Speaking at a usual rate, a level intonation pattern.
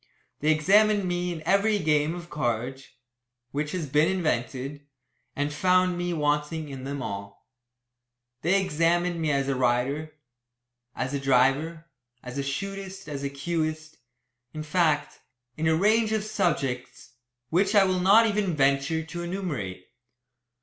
No: average, 145 wpm; average, 4.6 semitones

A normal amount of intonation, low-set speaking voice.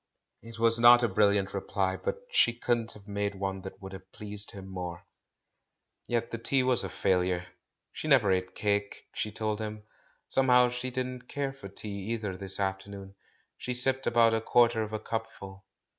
Yes: average, 3.5 semitones; low, 105 Hz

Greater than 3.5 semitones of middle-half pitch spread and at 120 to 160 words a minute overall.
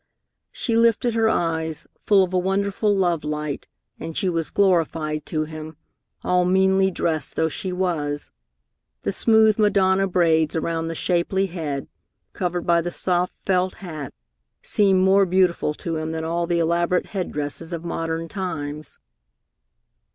No: average, 2.9 semitones; average, 150 wpm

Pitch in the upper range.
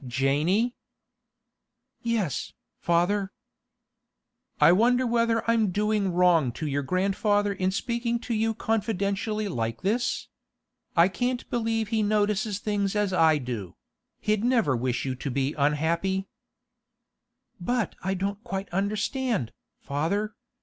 Yes: high, 200 Hz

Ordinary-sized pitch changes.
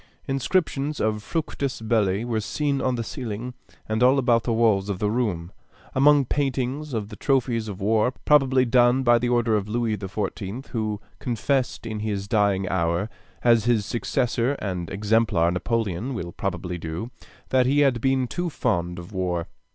Yes: average, 4.1 semitones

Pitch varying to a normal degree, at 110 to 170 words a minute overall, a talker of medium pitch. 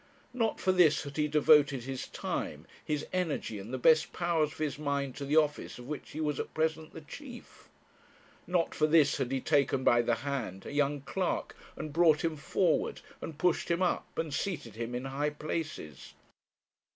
No: average, 3.0 semitones; average, 190 wpm; medium, 150 Hz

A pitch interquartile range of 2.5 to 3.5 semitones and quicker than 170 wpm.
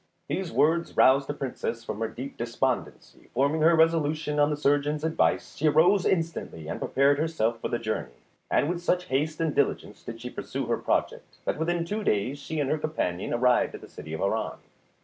No: average, 4.8 semitones; average, 200 wpm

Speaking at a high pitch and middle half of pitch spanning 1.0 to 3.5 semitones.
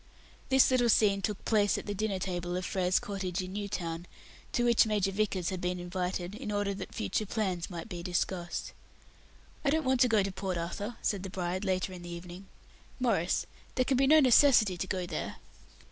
Yes: high, 195 Hz; average, 3.2 semitones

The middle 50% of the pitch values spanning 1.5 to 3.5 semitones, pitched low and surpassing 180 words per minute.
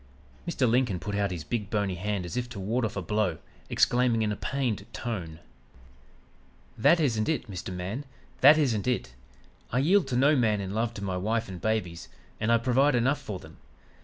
No: average, 4.2 semitones; low, 110 Hz; average, 195 wpm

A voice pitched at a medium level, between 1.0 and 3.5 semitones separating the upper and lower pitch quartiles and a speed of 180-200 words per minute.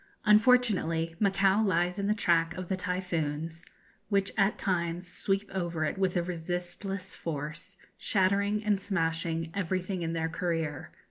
No: medium, 180 Hz; average, 3.1 semitones; average, 140 wpm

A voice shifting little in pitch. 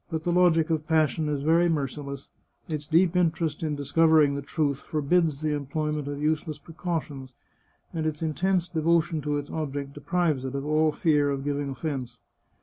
Yes: narrow, 2.3 semitones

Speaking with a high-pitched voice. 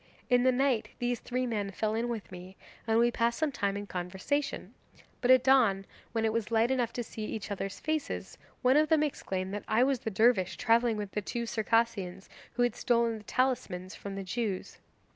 Yes: high, 230 Hz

